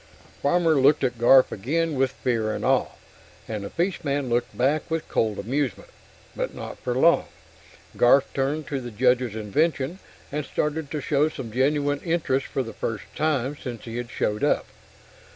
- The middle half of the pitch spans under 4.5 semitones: Yes, average, 3.9 semitones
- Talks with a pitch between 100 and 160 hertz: Yes, low, 135 Hz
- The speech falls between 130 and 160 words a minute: No, average, 170 wpm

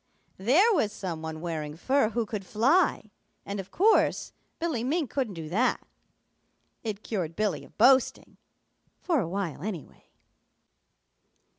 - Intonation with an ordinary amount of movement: No, wide, 6.9 semitones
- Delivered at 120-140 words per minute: Yes, slow, 135 wpm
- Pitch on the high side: Yes, high, 215 Hz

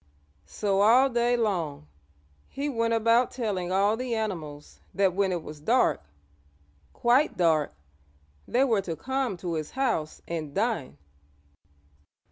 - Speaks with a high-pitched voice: Yes, high, 205 Hz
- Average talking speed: No, slow, 130 wpm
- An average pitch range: No, wide, 6.0 semitones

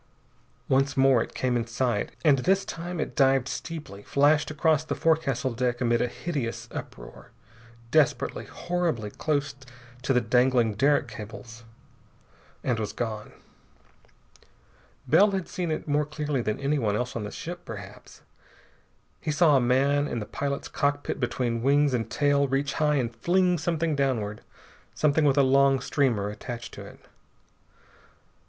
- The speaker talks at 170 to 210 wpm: No, average, 150 wpm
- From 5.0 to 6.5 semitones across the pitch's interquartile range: No, average, 4.1 semitones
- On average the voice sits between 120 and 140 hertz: Yes, low, 135 Hz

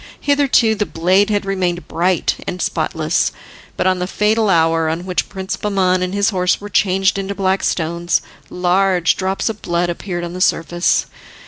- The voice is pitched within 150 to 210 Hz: Yes, medium, 185 Hz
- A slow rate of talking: No, average, 175 wpm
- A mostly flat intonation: Yes, narrow, 2.2 semitones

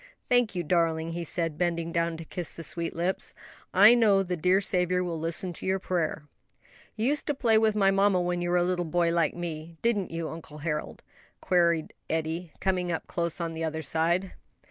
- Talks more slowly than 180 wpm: No, fast, 205 wpm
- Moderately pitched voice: Yes, medium, 175 Hz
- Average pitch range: No, narrow, 2.2 semitones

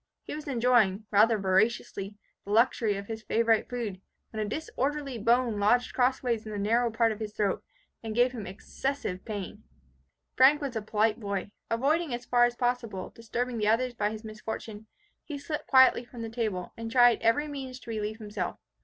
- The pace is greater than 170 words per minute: Yes, average, 185 wpm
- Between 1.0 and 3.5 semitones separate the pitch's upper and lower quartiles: Yes, average, 2.7 semitones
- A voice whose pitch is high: Yes, high, 230 Hz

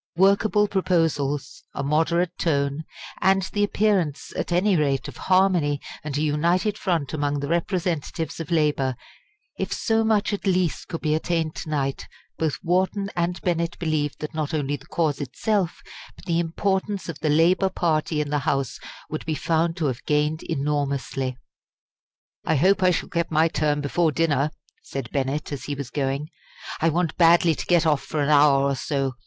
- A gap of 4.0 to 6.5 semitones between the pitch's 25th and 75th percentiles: No, average, 3.4 semitones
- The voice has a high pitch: No, medium, 160 Hz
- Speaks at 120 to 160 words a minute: No, average, 175 wpm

